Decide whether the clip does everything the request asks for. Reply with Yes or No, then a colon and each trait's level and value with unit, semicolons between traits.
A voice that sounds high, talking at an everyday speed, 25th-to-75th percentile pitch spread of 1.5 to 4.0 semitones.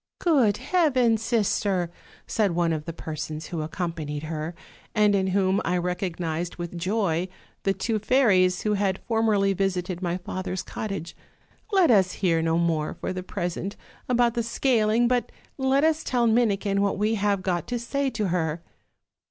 No: high, 195 Hz; average, 160 wpm; average, 4.5 semitones